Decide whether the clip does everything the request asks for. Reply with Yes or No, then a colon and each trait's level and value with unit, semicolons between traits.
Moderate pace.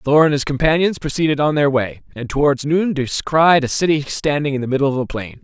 No: fast, 230 wpm